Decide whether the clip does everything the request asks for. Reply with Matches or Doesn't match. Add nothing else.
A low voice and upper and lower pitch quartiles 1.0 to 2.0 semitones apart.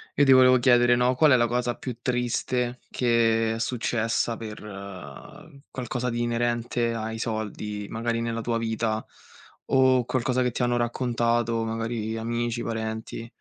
Matches